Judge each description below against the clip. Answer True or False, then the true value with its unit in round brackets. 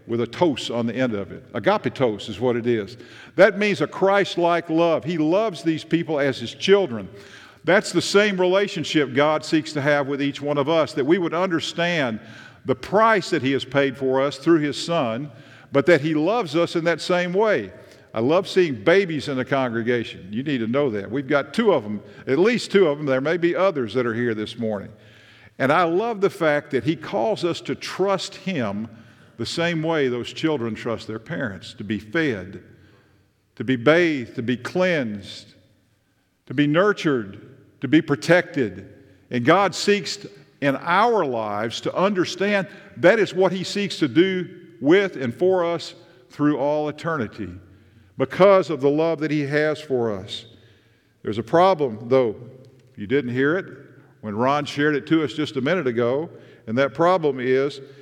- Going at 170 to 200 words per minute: True (190 wpm)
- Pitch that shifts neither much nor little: False (6.2 semitones)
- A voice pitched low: False (145 Hz)